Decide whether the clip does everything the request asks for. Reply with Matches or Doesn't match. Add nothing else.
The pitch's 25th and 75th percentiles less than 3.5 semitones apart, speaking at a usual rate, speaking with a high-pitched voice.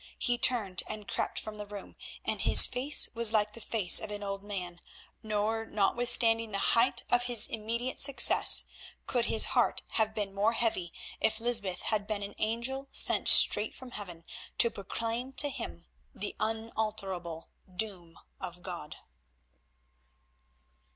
Matches